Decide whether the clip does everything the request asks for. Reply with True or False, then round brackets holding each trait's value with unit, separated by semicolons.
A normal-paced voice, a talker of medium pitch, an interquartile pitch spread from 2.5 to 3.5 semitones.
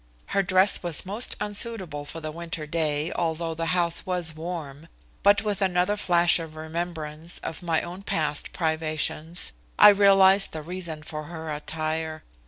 True (155 wpm; 165 Hz; 2.9 semitones)